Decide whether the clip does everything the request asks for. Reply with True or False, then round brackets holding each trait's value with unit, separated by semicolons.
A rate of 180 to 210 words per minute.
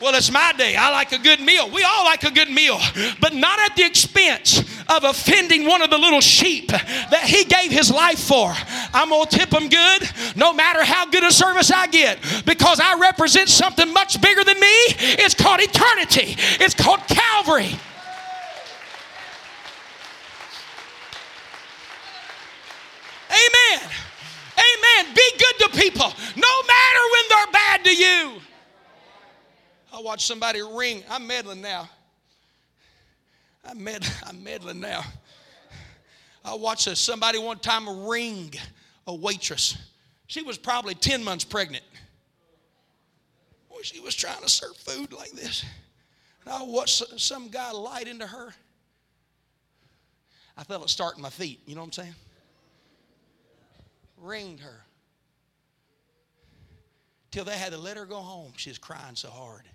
False (145 wpm)